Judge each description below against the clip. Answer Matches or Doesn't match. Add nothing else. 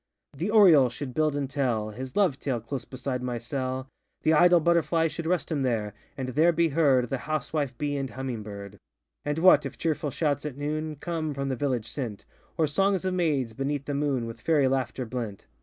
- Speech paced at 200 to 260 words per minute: Matches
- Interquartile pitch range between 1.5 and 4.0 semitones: Matches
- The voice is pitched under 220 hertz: Matches